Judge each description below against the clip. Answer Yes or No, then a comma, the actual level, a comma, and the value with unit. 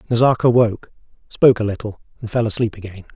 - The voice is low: Yes, low, 110 Hz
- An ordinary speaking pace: Yes, average, 170 wpm